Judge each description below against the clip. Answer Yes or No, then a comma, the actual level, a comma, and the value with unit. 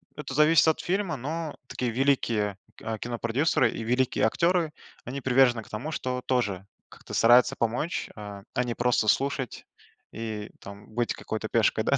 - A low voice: Yes, low, 125 Hz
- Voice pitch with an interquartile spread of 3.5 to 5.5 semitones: Yes, average, 3.9 semitones